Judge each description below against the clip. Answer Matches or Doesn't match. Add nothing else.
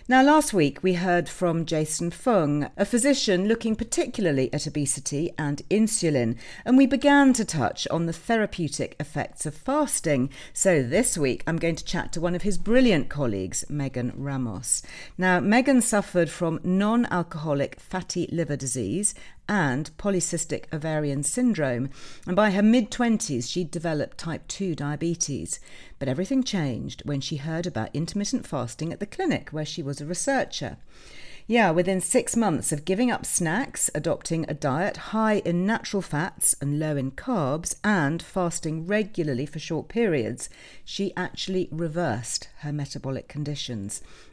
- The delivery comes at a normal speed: Matches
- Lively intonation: Matches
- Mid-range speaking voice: Matches